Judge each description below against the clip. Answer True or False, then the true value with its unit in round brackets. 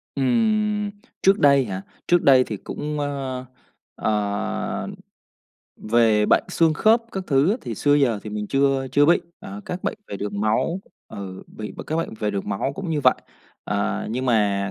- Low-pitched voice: True (130 Hz)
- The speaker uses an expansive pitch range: True (6.7 semitones)